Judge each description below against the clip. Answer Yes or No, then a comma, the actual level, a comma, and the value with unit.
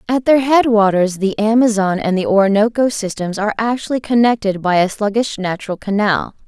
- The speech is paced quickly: No, average, 160 wpm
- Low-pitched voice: No, high, 215 Hz